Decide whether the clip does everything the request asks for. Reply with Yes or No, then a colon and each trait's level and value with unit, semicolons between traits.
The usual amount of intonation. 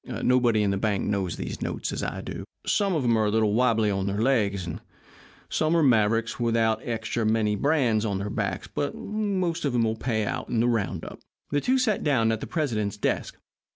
Yes: average, 4.1 semitones